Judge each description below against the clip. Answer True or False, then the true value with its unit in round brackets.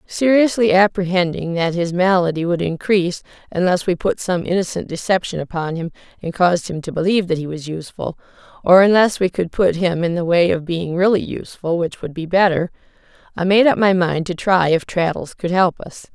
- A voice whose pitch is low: False (180 Hz)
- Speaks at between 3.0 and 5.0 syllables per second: False (5.4 syllables/s)